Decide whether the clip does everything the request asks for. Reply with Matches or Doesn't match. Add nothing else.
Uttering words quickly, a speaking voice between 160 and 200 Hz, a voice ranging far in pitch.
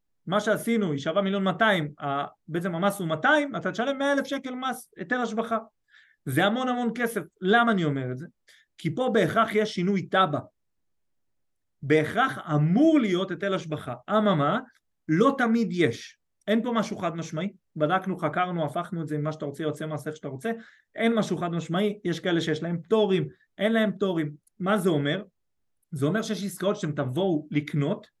Matches